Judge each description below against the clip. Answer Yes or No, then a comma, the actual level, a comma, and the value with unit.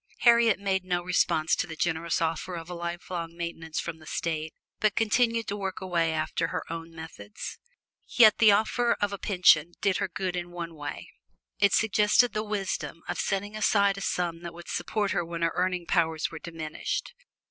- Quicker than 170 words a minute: Yes, average, 190 wpm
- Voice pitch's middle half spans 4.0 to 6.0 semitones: No, average, 3.4 semitones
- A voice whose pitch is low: No, medium, 175 Hz